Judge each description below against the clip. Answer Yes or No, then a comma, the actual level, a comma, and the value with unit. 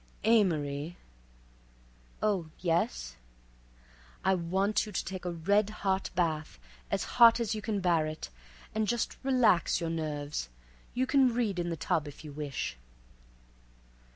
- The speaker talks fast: No, average, 140 wpm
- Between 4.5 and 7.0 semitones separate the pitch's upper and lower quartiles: Yes, wide, 5.5 semitones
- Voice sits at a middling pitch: Yes, medium, 180 Hz